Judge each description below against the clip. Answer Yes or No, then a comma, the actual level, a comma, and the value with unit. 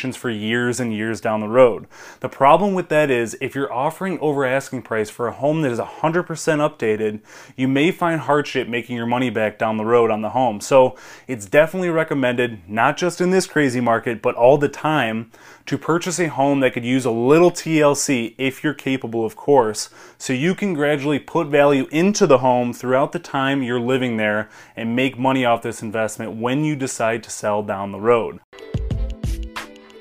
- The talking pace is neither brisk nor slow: Yes, average, 195 wpm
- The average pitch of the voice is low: Yes, low, 130 Hz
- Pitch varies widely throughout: No, average, 4.4 semitones